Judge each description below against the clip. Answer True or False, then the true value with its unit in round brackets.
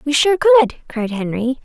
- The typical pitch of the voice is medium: False (260 Hz)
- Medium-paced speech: True (185 wpm)